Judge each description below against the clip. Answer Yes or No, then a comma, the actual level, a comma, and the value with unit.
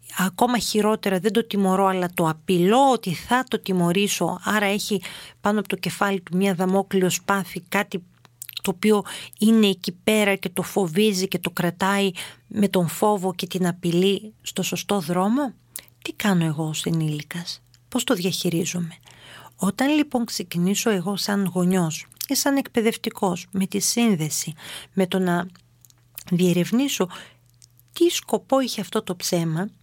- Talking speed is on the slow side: No, average, 145 wpm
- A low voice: No, high, 190 Hz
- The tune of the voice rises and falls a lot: No, average, 3.3 semitones